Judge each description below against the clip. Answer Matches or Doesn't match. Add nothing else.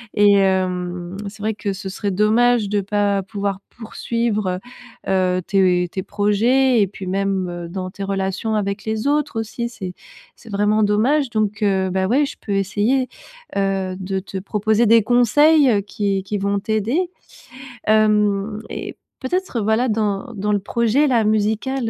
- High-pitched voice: Matches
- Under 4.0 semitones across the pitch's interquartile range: Matches